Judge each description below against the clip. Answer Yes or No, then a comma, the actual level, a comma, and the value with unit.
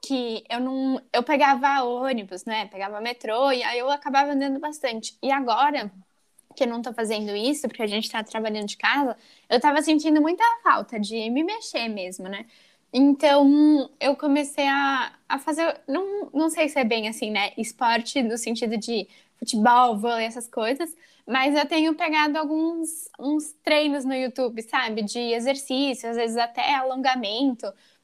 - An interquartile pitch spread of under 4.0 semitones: No, average, 4.4 semitones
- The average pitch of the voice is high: Yes, very high, 265 Hz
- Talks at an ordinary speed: Yes, average, 165 wpm